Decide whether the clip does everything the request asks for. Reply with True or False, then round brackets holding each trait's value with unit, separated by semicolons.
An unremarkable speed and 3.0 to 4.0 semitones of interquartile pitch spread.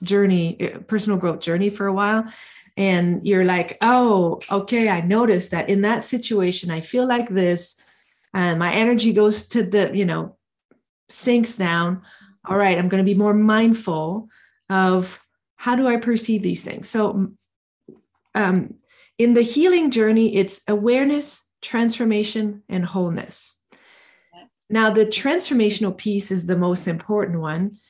True (145 wpm; 3.5 semitones)